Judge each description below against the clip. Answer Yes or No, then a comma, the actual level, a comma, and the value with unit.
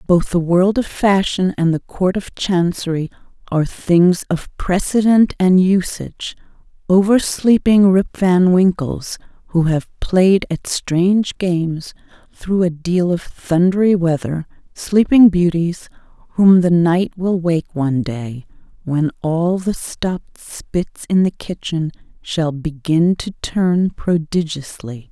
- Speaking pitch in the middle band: Yes, medium, 175 Hz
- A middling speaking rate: No, slow, 130 wpm